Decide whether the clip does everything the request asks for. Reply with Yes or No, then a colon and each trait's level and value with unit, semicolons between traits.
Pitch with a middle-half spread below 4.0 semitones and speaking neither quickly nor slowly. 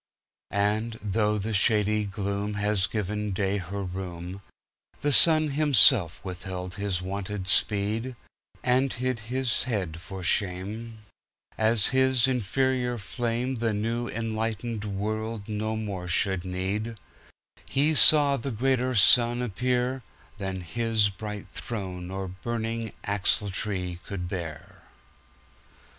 No: average, 3.4 semitones; slow, 100 wpm